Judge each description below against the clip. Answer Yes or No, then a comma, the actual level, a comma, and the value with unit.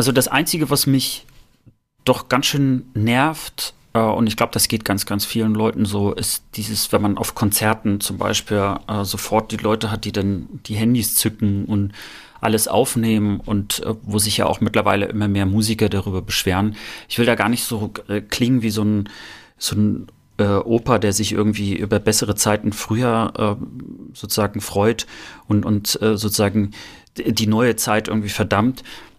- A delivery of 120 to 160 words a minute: No, average, 175 wpm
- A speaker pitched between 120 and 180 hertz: No, low, 110 Hz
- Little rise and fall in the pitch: Yes, narrow, 1.8 semitones